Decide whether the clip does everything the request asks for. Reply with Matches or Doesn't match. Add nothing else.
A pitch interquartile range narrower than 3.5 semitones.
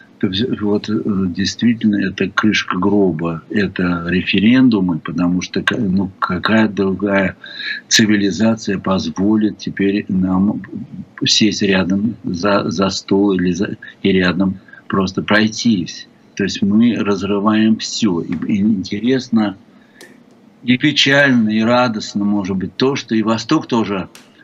Matches